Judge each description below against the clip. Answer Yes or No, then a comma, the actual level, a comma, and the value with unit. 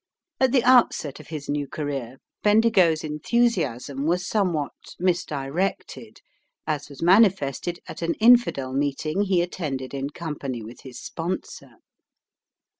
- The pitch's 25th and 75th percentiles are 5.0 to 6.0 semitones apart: Yes, average, 5.3 semitones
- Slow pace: Yes, slow, 120 wpm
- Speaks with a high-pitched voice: No, medium, 155 Hz